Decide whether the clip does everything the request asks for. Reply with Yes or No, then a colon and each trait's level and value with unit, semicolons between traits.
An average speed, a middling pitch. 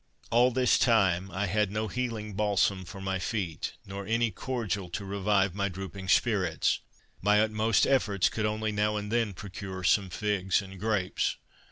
No: average, 165 wpm; low, 105 Hz